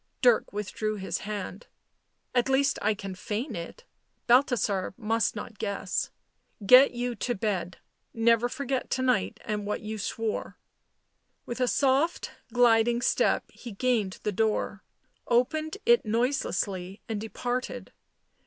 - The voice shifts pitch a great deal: No, average, 3.4 semitones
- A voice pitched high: Yes, high, 225 Hz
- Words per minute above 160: No, average, 145 wpm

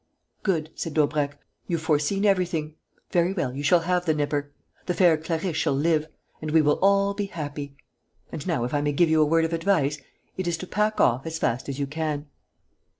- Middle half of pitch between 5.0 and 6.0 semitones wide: No, average, 3.3 semitones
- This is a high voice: No, medium, 160 Hz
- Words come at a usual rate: No, fast, 210 wpm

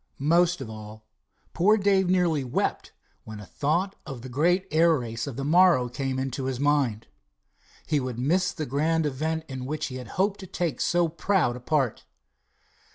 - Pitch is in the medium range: Yes, medium, 145 Hz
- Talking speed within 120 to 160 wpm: No, average, 180 wpm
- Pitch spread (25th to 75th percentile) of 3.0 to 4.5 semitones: No, average, 5.3 semitones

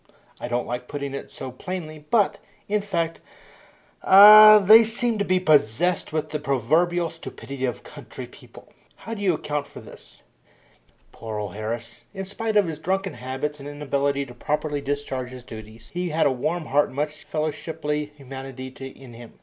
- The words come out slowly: No, average, 175 wpm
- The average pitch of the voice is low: No, medium, 150 Hz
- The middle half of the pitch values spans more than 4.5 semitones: Yes, average, 5.2 semitones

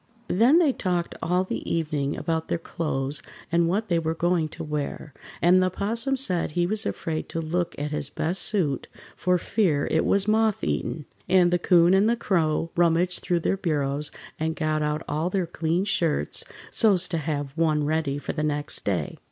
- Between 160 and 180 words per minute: No, average, 190 wpm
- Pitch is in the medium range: Yes, medium, 170 Hz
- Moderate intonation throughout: Yes, average, 3.2 semitones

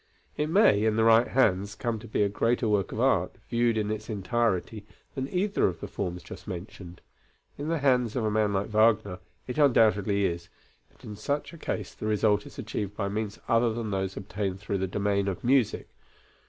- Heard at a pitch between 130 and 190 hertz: No, low, 105 Hz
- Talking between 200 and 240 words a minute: Yes, fast, 205 wpm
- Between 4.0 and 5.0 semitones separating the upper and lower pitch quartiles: No, average, 3.0 semitones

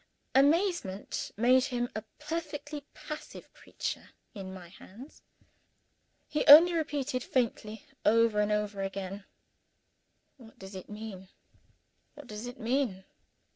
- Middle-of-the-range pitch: No, high, 230 Hz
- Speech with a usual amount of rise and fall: No, wide, 6.0 semitones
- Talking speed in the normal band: No, slow, 115 wpm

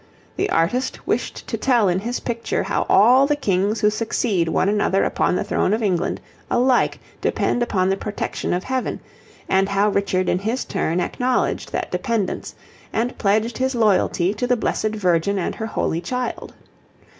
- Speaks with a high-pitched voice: Yes, high, 210 Hz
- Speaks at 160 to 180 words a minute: Yes, average, 170 wpm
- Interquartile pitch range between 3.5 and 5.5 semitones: Yes, average, 4.2 semitones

